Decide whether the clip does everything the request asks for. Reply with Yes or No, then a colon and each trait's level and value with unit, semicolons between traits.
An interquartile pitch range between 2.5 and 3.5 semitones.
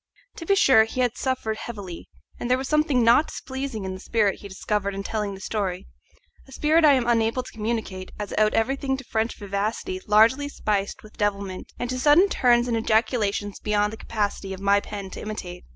No: average, 4.0 semitones